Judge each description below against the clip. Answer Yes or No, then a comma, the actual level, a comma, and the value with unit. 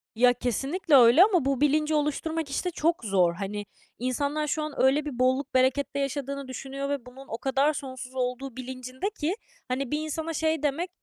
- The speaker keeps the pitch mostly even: No, average, 3.1 semitones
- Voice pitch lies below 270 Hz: No, very high, 275 Hz